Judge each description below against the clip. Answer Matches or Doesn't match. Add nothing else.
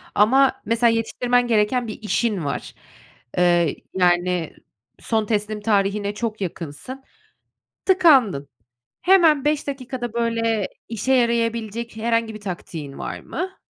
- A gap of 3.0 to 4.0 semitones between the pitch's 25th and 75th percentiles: Matches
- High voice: Matches